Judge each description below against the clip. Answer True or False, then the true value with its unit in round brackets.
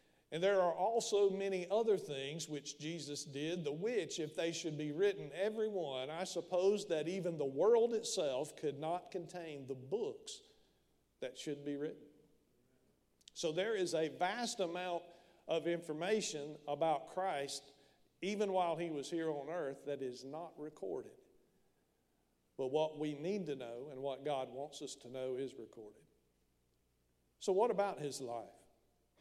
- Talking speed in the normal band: True (155 wpm)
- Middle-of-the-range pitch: True (155 Hz)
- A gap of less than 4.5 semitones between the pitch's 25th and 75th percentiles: False (4.8 semitones)